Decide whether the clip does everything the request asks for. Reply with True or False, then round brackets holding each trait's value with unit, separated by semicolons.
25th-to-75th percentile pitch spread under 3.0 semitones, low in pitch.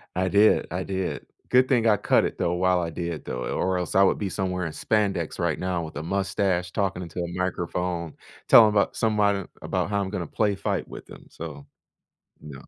True (2.6 semitones; 90 Hz)